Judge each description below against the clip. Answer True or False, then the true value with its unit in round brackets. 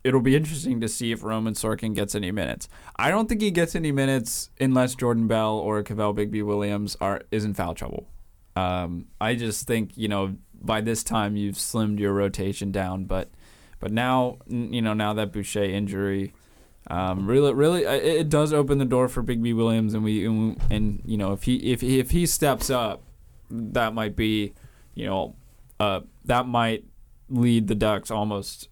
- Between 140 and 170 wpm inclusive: False (190 wpm)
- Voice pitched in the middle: False (110 Hz)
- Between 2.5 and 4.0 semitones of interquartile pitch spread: True (3.5 semitones)